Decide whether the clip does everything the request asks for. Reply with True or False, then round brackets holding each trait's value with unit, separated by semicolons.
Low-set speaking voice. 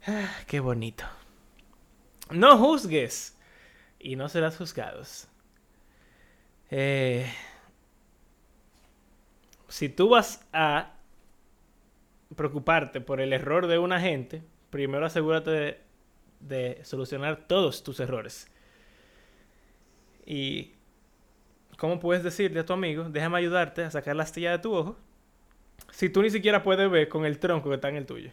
False (160 Hz)